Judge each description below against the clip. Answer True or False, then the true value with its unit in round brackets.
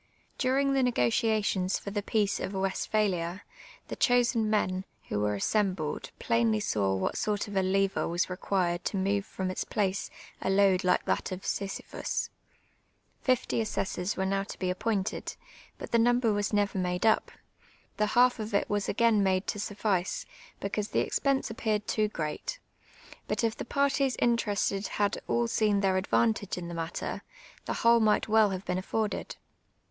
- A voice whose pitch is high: True (205 Hz)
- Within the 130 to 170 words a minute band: True (165 wpm)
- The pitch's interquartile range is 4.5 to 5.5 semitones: False (2.9 semitones)